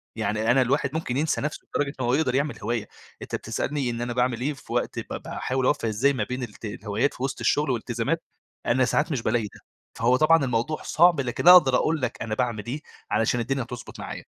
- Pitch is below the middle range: Yes, low, 125 Hz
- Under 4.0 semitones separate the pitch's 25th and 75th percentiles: Yes, average, 3.3 semitones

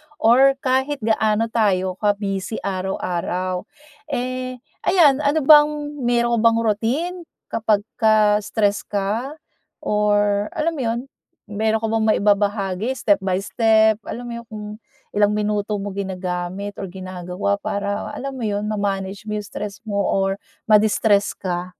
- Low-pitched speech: No, high, 210 Hz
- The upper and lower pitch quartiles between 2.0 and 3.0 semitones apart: Yes, narrow, 2.4 semitones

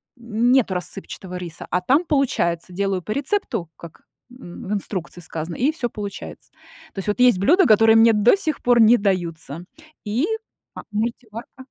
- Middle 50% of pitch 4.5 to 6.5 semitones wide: Yes, wide, 5.4 semitones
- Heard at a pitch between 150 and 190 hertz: No, high, 215 Hz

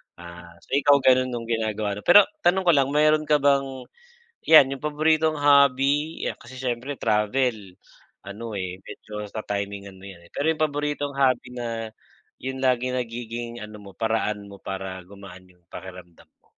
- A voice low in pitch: Yes, low, 120 Hz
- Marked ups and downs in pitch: Yes, wide, 5.7 semitones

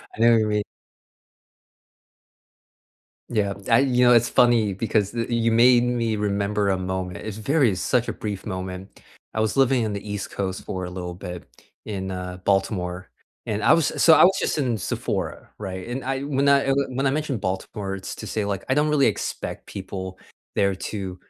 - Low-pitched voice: Yes, low, 105 Hz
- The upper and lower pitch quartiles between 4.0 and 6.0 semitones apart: Yes, average, 4.3 semitones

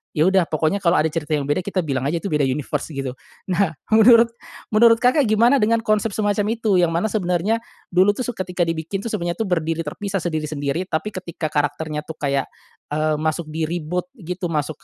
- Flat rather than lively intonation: No, average, 4.8 semitones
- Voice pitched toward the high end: No, medium, 175 Hz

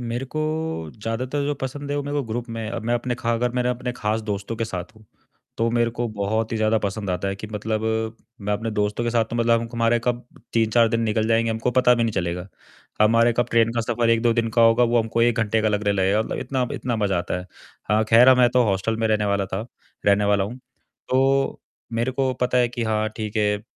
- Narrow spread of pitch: Yes, narrow, 2.1 semitones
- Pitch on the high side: No, low, 115 Hz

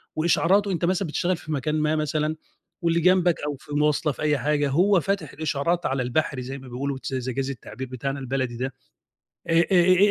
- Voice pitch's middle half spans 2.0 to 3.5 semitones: No, average, 4.2 semitones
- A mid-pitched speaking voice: Yes, medium, 150 Hz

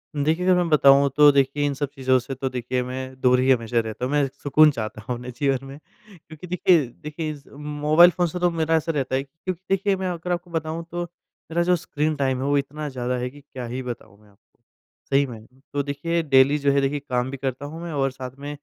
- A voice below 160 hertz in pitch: Yes, medium, 140 Hz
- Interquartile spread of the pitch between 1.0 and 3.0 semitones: No, average, 3.4 semitones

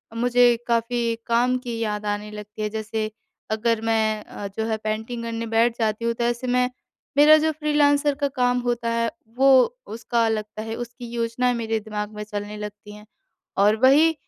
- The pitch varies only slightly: Yes, narrow, 2.3 semitones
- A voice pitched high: Yes, high, 230 Hz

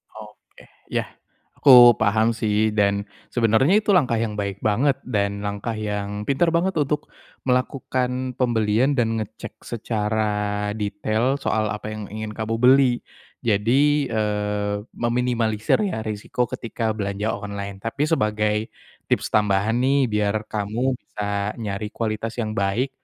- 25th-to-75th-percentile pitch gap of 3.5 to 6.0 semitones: No, average, 3.1 semitones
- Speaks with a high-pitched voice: No, low, 110 Hz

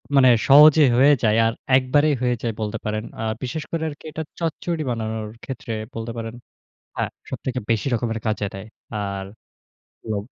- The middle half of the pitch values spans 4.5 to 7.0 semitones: Yes, average, 4.8 semitones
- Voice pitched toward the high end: No, low, 120 Hz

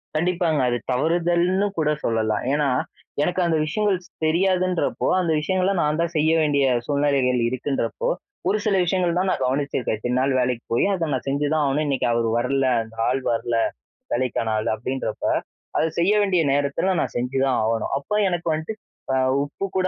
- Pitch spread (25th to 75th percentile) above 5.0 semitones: Yes, wide, 5.4 semitones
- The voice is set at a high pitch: No, medium, 150 Hz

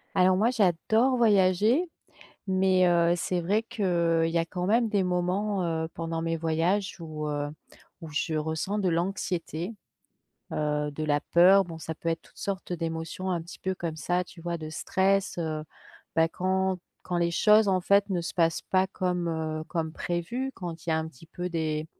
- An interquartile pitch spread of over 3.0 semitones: No, average, 2.7 semitones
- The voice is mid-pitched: Yes, medium, 175 Hz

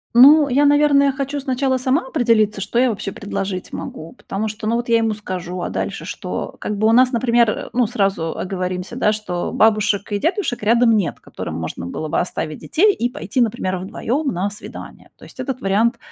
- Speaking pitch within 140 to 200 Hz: No, high, 225 Hz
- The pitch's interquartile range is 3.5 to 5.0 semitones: Yes, average, 4.7 semitones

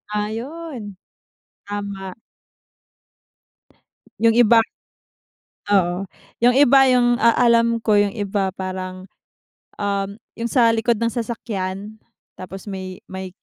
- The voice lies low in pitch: No, high, 210 Hz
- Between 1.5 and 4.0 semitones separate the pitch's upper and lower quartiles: Yes, average, 3.3 semitones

